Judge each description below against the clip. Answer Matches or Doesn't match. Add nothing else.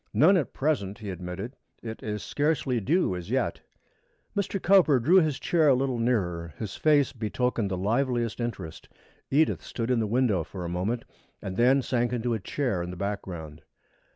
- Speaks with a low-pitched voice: Matches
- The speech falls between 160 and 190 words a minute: Matches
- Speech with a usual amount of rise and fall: Doesn't match